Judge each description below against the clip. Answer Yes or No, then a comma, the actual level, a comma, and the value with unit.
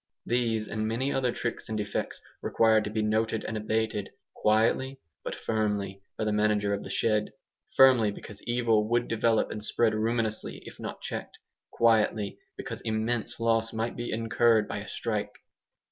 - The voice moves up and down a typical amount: No, narrow, 1.4 semitones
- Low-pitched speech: Yes, low, 110 Hz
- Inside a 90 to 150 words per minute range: No, average, 160 wpm